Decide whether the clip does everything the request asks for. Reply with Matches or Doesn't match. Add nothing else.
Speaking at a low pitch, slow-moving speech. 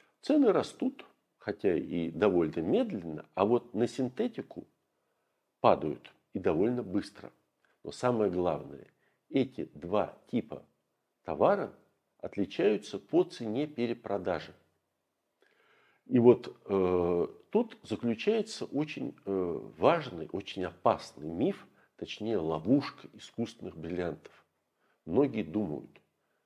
Matches